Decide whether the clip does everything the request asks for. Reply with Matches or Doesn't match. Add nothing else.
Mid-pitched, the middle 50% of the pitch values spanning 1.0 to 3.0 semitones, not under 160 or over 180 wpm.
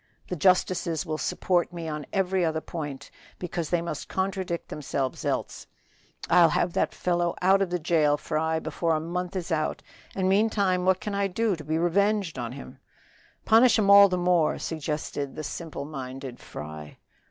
Doesn't match